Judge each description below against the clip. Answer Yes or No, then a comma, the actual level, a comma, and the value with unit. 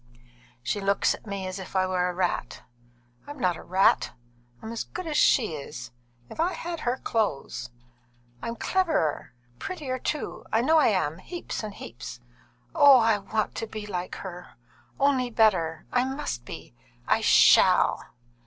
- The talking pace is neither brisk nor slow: Yes, average, 165 wpm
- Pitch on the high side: Yes, high, 215 Hz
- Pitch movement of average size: No, wide, 6.7 semitones